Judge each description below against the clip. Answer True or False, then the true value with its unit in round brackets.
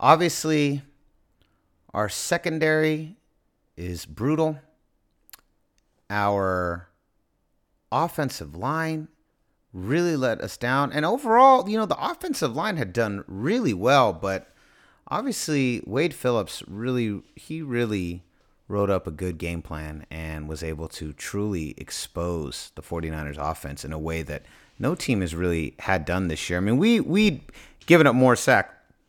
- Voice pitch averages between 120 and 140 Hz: False (110 Hz)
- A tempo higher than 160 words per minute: False (135 wpm)